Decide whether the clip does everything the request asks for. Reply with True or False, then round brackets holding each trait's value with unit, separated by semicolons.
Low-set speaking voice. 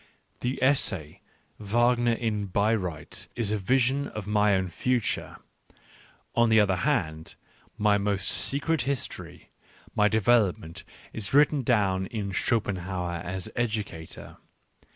True (105 Hz)